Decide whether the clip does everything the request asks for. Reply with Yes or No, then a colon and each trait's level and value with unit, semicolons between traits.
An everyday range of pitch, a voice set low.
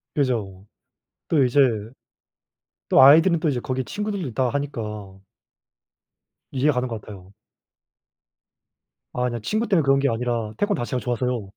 Yes: average, 3.8 semitones; low, 125 Hz